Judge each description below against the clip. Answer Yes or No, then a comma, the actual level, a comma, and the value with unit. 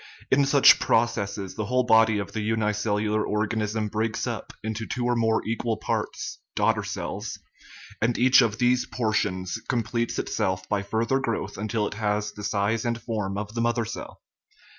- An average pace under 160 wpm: No, average, 165 wpm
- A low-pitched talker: Yes, low, 110 Hz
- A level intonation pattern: Yes, narrow, 2.0 semitones